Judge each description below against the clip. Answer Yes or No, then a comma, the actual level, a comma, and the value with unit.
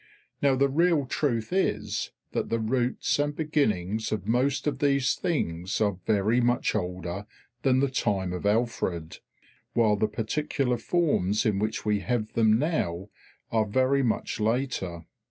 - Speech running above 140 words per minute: Yes, average, 150 wpm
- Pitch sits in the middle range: No, low, 115 Hz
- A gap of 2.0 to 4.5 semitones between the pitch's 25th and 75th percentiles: No, average, 4.9 semitones